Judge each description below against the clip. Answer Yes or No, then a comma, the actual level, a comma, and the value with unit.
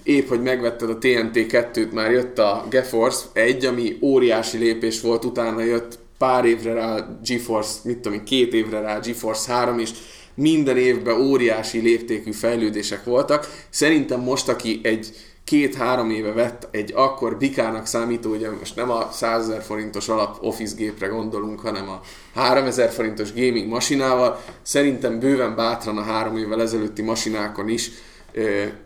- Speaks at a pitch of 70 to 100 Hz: No, low, 115 Hz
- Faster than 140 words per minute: Yes, average, 150 wpm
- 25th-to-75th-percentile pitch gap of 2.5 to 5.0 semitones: No, narrow, 2.1 semitones